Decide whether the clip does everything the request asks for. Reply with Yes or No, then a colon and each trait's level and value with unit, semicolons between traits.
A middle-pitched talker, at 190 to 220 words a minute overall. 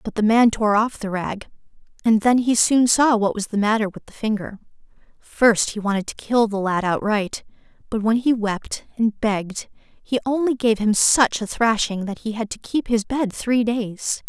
No: high, 220 Hz; fast, 205 wpm